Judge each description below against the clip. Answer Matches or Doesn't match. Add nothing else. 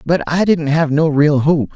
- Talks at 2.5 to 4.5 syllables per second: Matches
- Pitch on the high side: Doesn't match